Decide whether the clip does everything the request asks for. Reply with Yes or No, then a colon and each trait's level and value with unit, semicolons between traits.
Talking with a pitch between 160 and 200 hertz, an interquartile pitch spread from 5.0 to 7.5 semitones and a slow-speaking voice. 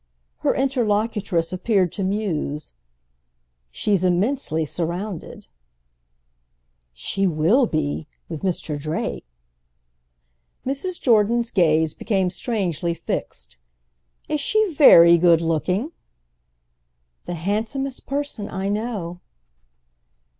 Yes: high, 190 Hz; wide, 5.6 semitones; slow, 85 wpm